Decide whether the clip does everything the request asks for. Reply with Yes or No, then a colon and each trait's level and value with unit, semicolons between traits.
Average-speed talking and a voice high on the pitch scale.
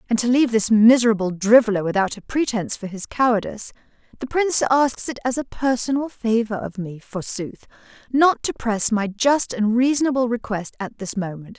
Yes: average, 175 wpm; high, 230 Hz